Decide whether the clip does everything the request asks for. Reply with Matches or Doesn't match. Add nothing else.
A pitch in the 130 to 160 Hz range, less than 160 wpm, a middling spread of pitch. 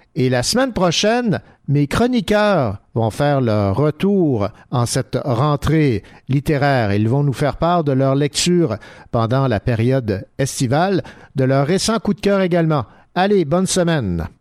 Doesn't match